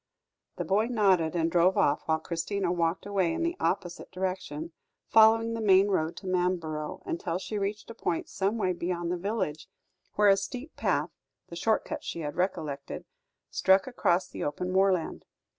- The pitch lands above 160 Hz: Yes, medium, 185 Hz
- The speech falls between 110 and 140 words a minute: No, average, 175 wpm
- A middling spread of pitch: Yes, average, 3.1 semitones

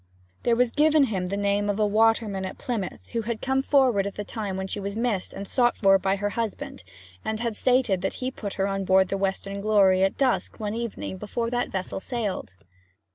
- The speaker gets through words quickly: Yes, fast, 220 wpm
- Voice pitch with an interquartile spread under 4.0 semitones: Yes, average, 3.4 semitones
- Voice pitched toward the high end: Yes, high, 205 Hz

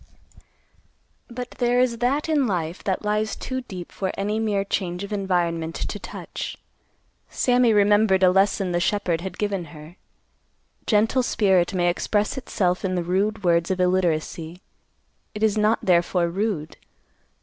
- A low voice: No, high, 195 Hz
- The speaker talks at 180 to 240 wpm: No, average, 150 wpm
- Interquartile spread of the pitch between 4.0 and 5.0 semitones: No, average, 3.4 semitones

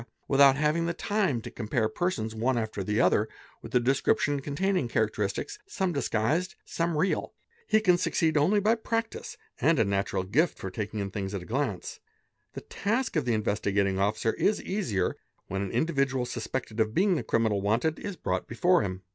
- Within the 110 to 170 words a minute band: No, average, 190 wpm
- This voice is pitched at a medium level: No, low, 125 Hz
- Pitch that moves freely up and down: Yes, wide, 8.2 semitones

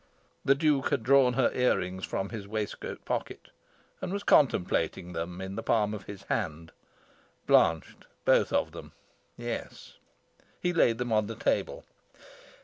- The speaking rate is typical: Yes, average, 150 wpm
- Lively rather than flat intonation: Yes, wide, 5.7 semitones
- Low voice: Yes, low, 110 Hz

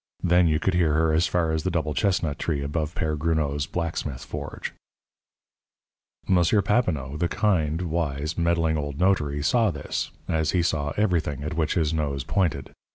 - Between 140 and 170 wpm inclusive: Yes, average, 165 wpm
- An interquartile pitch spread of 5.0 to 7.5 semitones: No, average, 2.9 semitones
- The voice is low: Yes, very low, 80 Hz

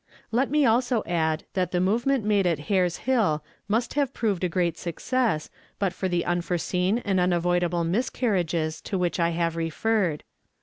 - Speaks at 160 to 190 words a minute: Yes, average, 165 wpm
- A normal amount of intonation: Yes, average, 4.6 semitones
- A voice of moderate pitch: Yes, medium, 180 Hz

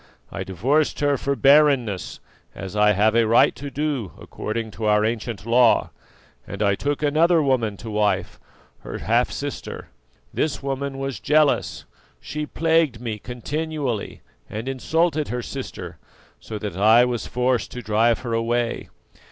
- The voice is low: Yes, low, 125 Hz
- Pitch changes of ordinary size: Yes, average, 4.6 semitones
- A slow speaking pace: No, average, 150 wpm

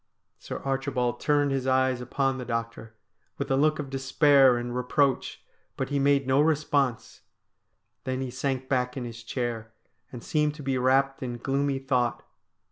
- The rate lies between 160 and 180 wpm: Yes, average, 165 wpm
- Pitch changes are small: Yes, narrow, 2.0 semitones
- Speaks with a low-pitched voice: Yes, low, 130 Hz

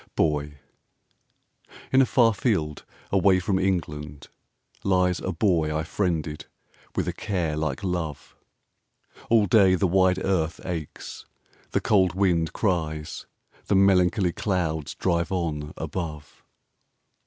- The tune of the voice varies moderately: Yes, average, 3.6 semitones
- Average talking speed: No, slow, 120 wpm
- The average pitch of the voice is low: Yes, very low, 90 Hz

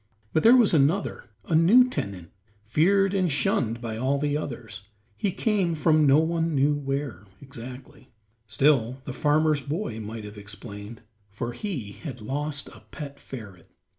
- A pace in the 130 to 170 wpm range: Yes, average, 155 wpm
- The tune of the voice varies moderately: No, wide, 5.7 semitones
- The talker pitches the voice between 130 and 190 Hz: Yes, medium, 140 Hz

